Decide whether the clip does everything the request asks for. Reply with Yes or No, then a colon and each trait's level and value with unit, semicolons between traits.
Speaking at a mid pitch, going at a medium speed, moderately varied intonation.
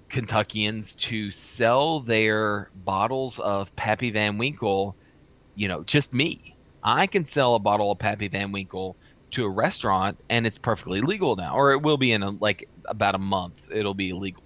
No: low, 105 Hz; average, 180 wpm; average, 3.0 semitones